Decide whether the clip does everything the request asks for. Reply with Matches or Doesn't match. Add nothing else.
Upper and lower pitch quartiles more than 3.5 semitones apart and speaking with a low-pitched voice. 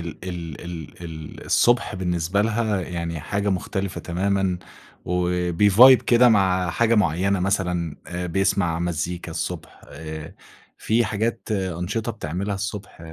Doesn't match